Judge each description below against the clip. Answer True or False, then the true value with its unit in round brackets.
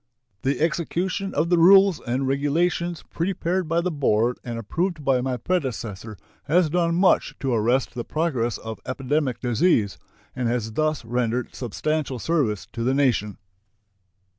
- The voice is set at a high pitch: False (135 Hz)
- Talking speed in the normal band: True (145 wpm)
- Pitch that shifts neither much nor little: False (6.0 semitones)